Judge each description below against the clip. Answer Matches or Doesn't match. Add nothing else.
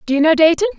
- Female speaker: Matches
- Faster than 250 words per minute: Matches